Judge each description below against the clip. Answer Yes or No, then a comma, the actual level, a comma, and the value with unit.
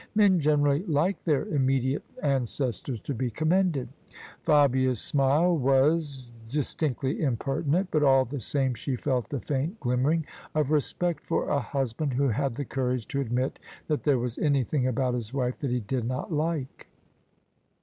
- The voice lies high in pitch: No, low, 135 Hz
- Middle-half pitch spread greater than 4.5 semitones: No, average, 2.9 semitones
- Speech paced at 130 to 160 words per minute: No, average, 175 wpm